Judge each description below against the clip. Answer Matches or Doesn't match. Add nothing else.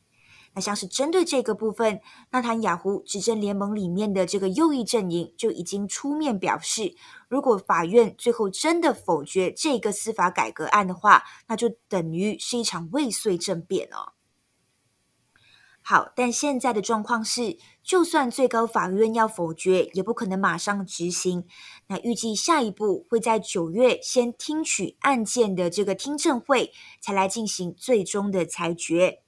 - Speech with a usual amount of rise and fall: Matches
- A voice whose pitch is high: Matches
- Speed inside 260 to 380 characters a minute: Doesn't match